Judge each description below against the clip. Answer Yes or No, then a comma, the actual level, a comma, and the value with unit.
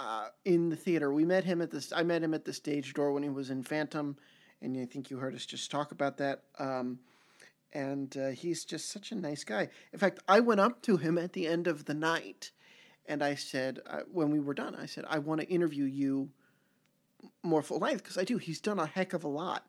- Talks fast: Yes, fast, 245 wpm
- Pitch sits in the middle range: Yes, medium, 150 Hz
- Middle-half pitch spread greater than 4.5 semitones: No, average, 3.6 semitones